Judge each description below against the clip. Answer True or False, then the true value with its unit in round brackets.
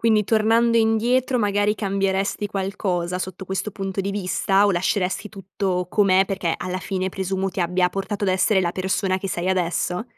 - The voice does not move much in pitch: True (1.9 semitones)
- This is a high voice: True (195 Hz)